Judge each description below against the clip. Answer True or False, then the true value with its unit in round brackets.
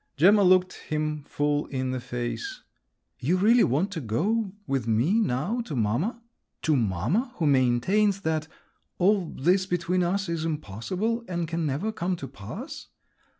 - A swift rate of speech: False (150 wpm)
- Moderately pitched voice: True (170 Hz)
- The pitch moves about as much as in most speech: False (6.5 semitones)